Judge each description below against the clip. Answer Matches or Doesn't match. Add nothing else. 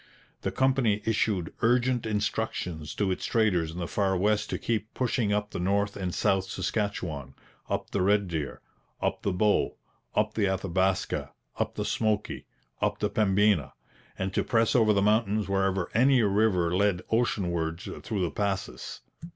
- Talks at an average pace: Matches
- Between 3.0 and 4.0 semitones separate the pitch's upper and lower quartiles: Doesn't match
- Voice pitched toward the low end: Matches